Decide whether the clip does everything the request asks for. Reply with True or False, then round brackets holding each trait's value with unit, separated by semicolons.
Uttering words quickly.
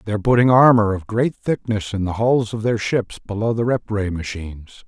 True (210 wpm)